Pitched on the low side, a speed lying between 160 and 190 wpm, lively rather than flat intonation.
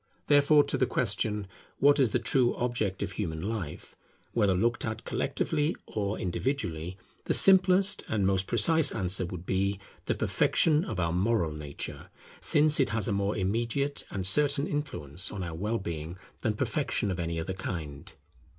Yes: low, 100 Hz; average, 165 wpm; wide, 6.4 semitones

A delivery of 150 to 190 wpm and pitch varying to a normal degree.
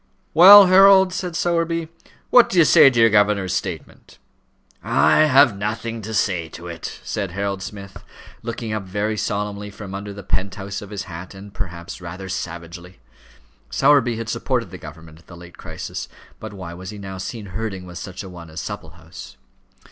Yes: average, 180 wpm; average, 3.9 semitones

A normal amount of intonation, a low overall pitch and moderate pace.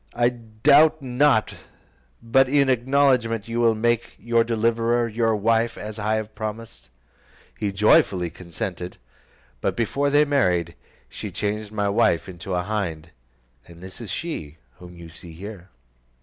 Yes: average, 4.0 semitones; low, 110 Hz; average, 145 wpm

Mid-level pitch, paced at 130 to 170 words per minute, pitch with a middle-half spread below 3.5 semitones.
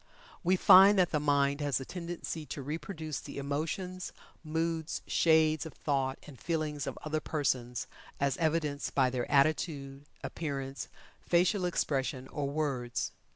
Yes: medium, 150 Hz; average, 140 wpm; average, 2.9 semitones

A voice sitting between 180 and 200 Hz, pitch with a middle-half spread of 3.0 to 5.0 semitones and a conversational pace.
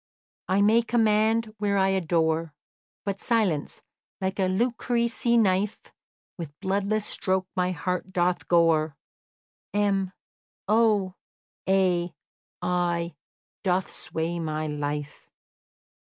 No: high, 190 Hz; average, 3.6 semitones; slow, 100 wpm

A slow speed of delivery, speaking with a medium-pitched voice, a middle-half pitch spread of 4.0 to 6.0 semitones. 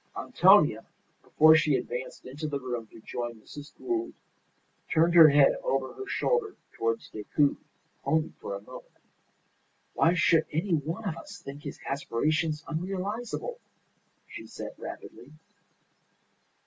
Yes: slow, 130 wpm; medium, 155 Hz; average, 4.4 semitones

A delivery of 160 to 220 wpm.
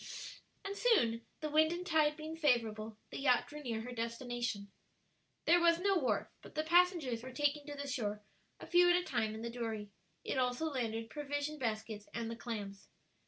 Yes: average, 190 wpm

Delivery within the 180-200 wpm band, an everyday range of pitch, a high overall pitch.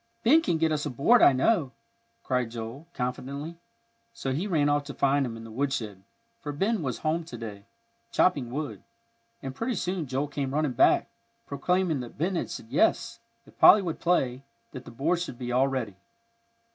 No: average, 190 wpm; average, 4.8 semitones; medium, 140 Hz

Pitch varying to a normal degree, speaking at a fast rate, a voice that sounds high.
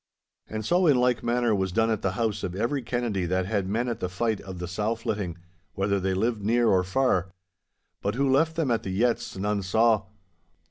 No: average, 4.0 semitones; fast, 215 wpm; low, 110 Hz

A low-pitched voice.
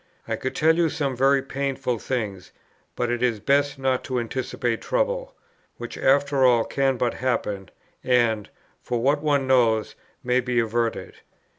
Yes: low, 130 Hz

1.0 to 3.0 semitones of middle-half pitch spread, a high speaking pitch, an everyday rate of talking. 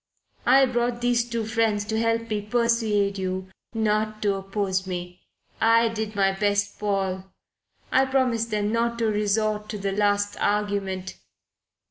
Yes: narrow, 2.4 semitones; high, 210 Hz; average, 145 wpm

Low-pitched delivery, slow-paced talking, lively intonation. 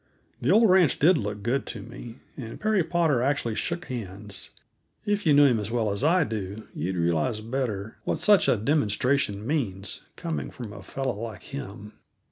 No: low, 120 Hz; average, 180 wpm; wide, 6.2 semitones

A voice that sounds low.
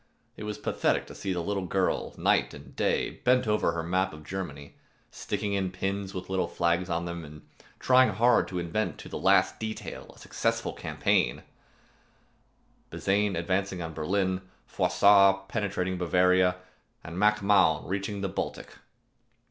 Yes: very low, 95 Hz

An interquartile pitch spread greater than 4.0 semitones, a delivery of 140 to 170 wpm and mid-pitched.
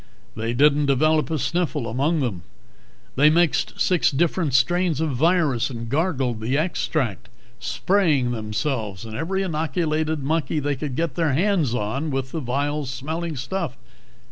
Yes: average, 4.4 semitones; average, 145 wpm; medium, 145 Hz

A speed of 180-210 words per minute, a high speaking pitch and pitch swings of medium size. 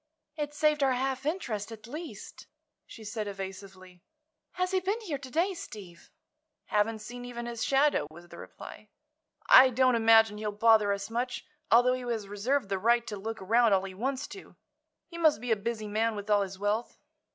Yes: average, 190 wpm; high, 225 Hz; average, 4.3 semitones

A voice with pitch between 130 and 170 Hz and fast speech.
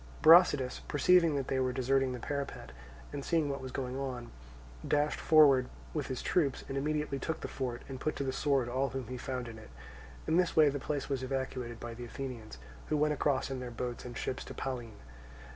Yes: low, 135 Hz; fast, 210 wpm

